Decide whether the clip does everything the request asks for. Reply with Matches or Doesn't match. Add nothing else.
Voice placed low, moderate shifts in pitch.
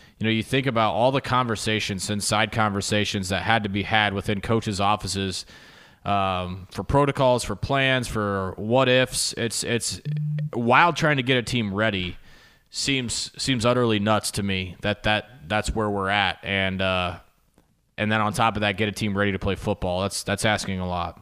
Matches